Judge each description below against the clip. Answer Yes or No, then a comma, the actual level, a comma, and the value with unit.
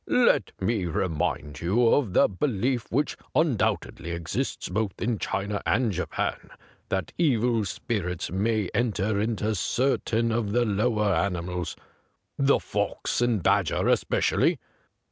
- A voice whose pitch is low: Yes, low, 105 Hz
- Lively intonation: No, average, 4.2 semitones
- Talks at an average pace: No, slow, 125 wpm